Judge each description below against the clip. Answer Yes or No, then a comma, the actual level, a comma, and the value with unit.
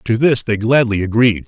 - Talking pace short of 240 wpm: Yes, fast, 205 wpm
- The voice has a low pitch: Yes, low, 115 Hz